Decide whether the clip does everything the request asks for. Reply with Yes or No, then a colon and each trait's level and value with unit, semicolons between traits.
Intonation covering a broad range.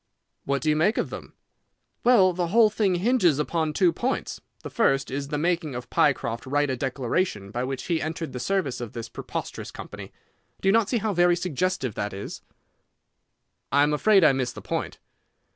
Yes: wide, 5.8 semitones